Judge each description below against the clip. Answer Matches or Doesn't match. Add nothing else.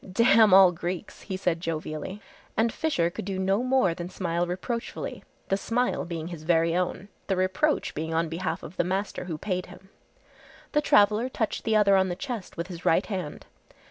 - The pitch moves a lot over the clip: Doesn't match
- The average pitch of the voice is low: Doesn't match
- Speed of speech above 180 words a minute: Matches